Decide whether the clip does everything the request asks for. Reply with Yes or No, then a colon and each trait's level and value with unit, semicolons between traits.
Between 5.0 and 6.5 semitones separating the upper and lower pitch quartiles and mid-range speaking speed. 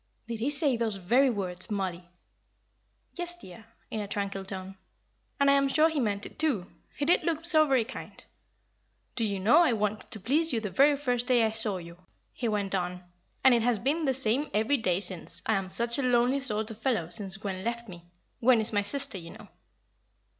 No: wide, 5.5 semitones; fast, 210 wpm